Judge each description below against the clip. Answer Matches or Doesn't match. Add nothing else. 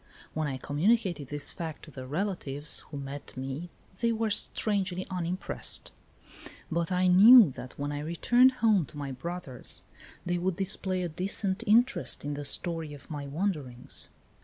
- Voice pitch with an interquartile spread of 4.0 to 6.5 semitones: Matches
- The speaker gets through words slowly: Doesn't match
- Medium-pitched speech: Matches